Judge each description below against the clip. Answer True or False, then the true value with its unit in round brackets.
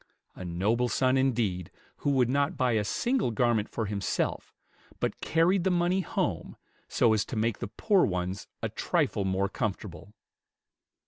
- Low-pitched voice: True (115 Hz)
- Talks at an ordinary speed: True (155 wpm)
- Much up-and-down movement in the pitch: True (6.0 semitones)